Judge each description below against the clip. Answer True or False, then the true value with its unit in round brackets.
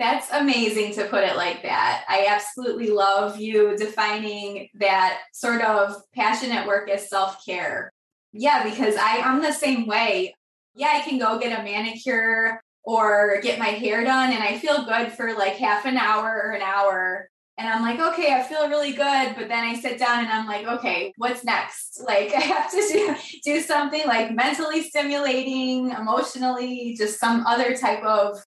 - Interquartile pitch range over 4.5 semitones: False (3.8 semitones)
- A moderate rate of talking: True (180 wpm)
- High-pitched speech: True (225 Hz)